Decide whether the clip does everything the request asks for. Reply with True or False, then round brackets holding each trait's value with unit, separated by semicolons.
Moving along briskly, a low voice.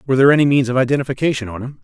True (260 wpm; 130 Hz)